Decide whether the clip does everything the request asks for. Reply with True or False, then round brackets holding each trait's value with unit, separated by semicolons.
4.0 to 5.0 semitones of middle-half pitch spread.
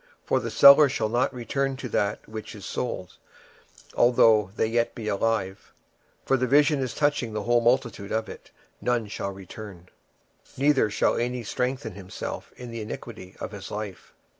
False (3.4 semitones)